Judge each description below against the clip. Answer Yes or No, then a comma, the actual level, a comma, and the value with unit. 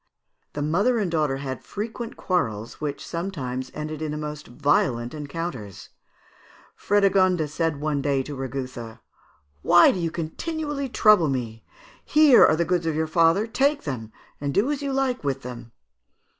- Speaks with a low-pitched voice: No, medium, 155 Hz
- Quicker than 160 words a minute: No, average, 155 wpm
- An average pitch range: No, wide, 6.5 semitones